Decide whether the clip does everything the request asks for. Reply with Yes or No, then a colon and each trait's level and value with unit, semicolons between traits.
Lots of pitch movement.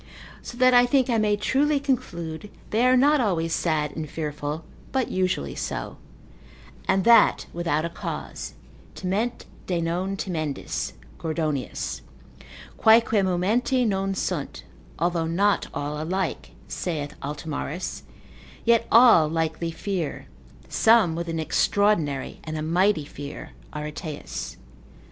Yes: wide, 5.8 semitones